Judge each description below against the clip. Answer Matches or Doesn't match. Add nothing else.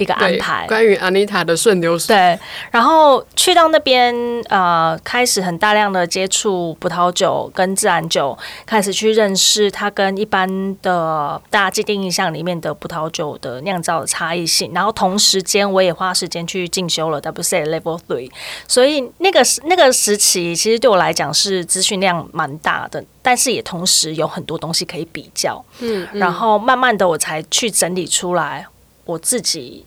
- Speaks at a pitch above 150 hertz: Matches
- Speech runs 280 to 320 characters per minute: Matches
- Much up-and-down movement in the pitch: Doesn't match